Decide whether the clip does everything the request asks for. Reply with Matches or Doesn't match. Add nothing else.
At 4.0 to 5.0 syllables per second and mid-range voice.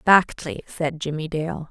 Matches